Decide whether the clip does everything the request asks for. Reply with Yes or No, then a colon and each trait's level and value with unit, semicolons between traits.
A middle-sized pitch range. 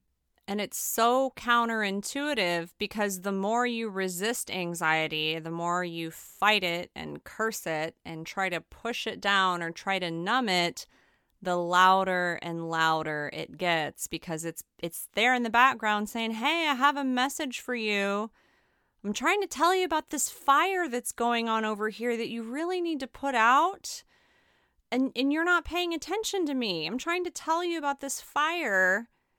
No: wide, 7.7 semitones